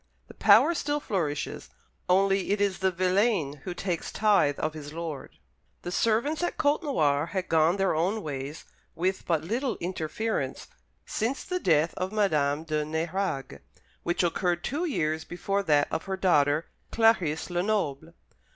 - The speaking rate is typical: Yes, average, 150 wpm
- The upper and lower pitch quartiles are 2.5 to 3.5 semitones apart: No, average, 4.6 semitones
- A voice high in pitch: No, medium, 180 Hz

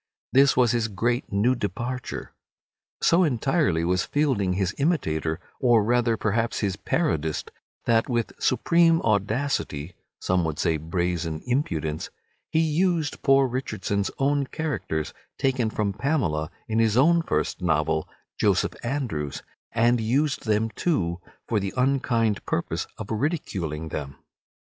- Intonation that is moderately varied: No, wide, 7.0 semitones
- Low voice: Yes, low, 115 Hz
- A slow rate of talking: Yes, slow, 130 wpm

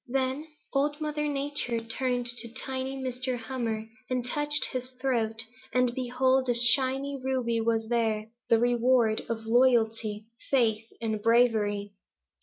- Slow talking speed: Yes, slow, 130 wpm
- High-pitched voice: Yes, high, 245 Hz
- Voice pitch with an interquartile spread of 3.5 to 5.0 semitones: No, narrow, 2.6 semitones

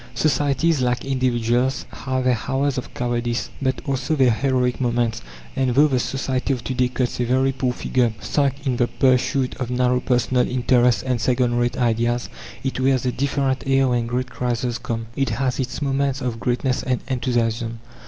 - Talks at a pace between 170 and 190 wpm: Yes, average, 180 wpm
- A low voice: Yes, low, 125 Hz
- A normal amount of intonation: No, narrow, 1.6 semitones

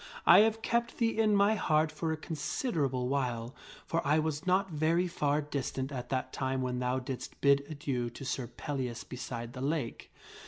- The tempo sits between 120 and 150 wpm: No, average, 185 wpm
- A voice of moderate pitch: Yes, medium, 145 Hz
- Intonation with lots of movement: No, average, 4.3 semitones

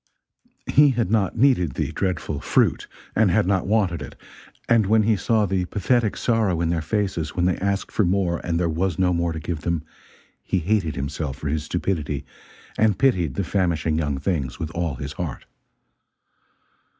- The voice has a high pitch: No, very low, 90 Hz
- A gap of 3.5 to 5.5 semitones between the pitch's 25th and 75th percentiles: Yes, average, 4.2 semitones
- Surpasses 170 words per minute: Yes, average, 180 wpm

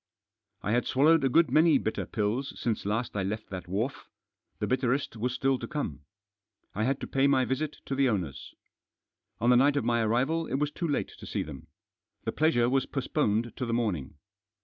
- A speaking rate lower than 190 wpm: No, fast, 205 wpm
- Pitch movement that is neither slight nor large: Yes, average, 4.2 semitones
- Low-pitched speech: Yes, low, 125 Hz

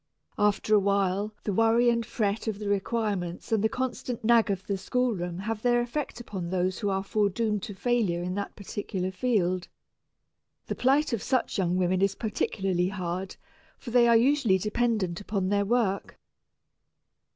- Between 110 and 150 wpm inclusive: No, average, 165 wpm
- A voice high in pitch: Yes, high, 205 Hz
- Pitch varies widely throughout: No, average, 3.7 semitones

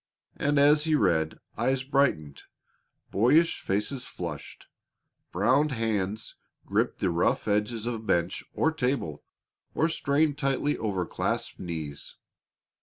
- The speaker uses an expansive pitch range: Yes, wide, 7.0 semitones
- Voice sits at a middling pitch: No, low, 120 Hz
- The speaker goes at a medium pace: No, slow, 115 wpm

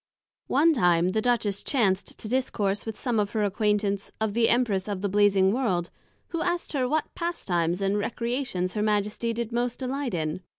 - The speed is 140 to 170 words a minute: No, average, 180 wpm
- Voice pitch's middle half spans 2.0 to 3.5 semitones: No, average, 4.0 semitones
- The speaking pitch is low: No, high, 210 Hz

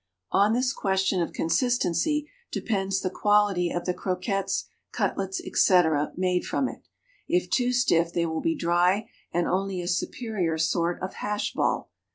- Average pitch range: Yes, average, 3.0 semitones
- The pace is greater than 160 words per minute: No, average, 155 wpm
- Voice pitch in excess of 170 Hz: Yes, high, 190 Hz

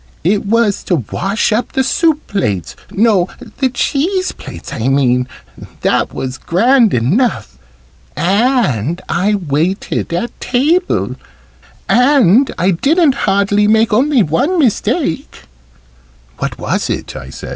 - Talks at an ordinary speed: No, slow, 125 wpm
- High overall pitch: Yes, high, 210 Hz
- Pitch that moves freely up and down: Yes, wide, 7.6 semitones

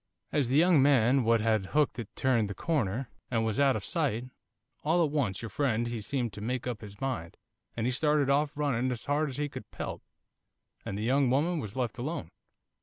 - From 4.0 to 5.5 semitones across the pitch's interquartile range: Yes, average, 4.3 semitones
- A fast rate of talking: Yes, fast, 215 wpm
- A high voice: No, low, 130 Hz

